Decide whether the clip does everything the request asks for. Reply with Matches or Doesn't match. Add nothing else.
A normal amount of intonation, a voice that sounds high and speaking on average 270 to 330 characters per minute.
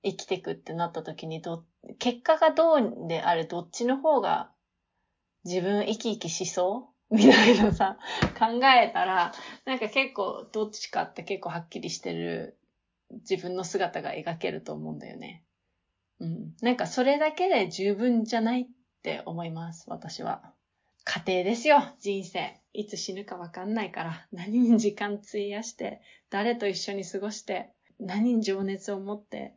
Matches